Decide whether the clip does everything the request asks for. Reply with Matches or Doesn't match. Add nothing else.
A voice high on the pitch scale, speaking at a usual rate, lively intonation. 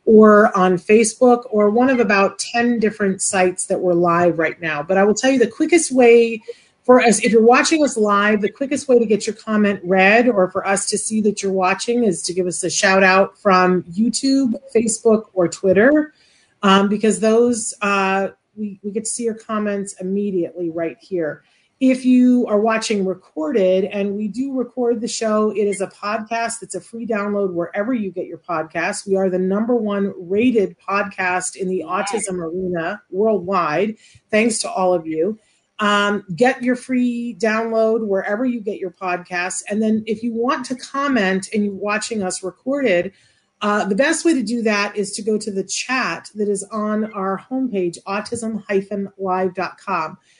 Doesn't match